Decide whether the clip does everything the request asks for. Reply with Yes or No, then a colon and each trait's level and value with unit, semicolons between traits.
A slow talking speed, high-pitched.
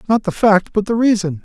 No: fast, 250 wpm; high, 205 Hz